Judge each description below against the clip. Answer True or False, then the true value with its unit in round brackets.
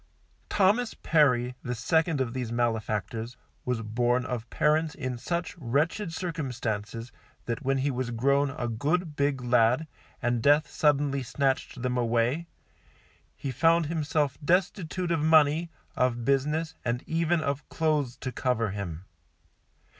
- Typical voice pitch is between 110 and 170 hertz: True (135 Hz)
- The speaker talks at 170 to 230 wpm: False (135 wpm)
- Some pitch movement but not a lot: True (4.6 semitones)